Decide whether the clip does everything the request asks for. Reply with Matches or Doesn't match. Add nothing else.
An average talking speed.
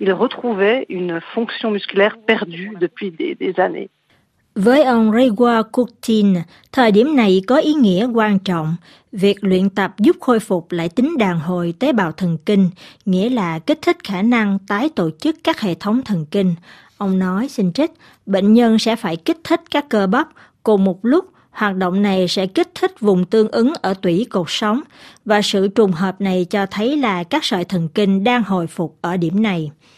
Matches